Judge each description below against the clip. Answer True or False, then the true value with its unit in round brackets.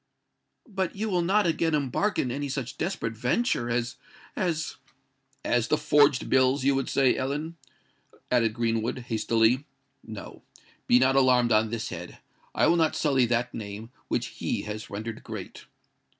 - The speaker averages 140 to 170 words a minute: True (150 wpm)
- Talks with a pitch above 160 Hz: False (130 Hz)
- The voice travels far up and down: False (4.7 semitones)